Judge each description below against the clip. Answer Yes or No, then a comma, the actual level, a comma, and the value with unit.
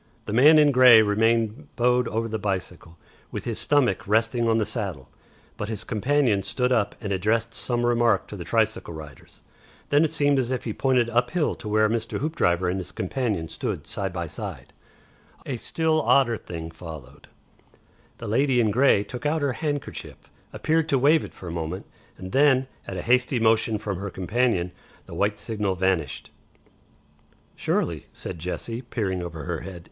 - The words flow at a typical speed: Yes, average, 180 wpm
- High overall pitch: No, low, 115 Hz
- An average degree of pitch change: Yes, average, 4.9 semitones